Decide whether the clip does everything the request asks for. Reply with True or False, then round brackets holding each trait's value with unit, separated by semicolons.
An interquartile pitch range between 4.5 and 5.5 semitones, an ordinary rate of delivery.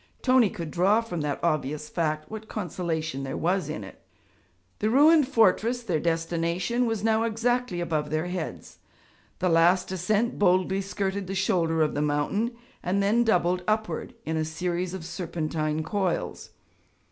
True (4.9 semitones; 155 wpm)